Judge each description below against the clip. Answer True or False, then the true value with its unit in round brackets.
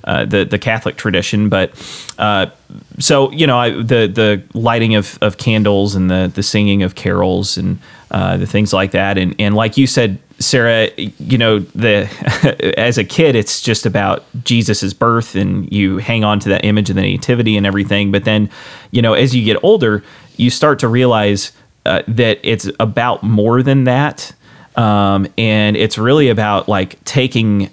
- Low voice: True (105 Hz)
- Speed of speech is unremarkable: True (180 wpm)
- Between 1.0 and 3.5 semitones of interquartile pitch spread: True (3.2 semitones)